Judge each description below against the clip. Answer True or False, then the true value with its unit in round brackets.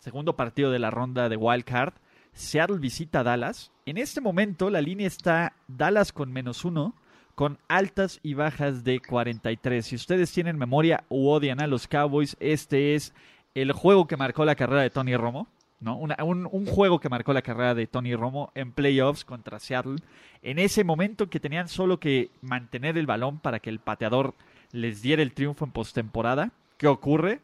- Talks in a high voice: False (140 Hz)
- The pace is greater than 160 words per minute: True (190 wpm)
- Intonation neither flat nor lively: True (4.7 semitones)